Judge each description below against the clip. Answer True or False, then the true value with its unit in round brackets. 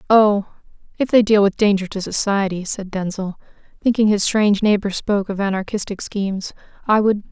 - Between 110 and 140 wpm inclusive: False (165 wpm)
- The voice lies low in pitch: False (205 Hz)